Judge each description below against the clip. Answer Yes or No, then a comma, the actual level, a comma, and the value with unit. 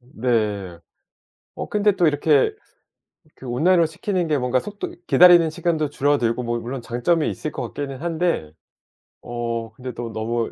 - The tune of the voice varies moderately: No, wide, 5.7 semitones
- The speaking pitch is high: No, low, 135 Hz